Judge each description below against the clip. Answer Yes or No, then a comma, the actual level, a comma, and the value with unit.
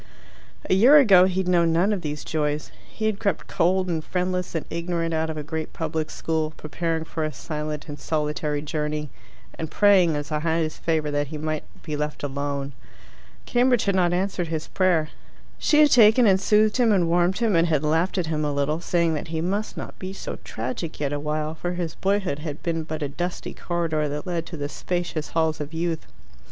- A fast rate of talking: Yes, fast, 210 wpm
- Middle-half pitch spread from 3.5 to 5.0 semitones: No, average, 3.1 semitones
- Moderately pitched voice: Yes, medium, 165 Hz